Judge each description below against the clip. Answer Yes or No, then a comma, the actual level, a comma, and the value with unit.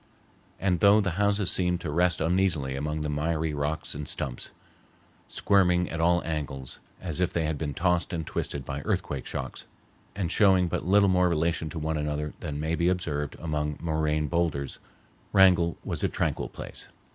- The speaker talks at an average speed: Yes, average, 175 wpm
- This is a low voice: Yes, very low, 80 Hz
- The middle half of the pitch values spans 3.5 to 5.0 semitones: No, average, 3.0 semitones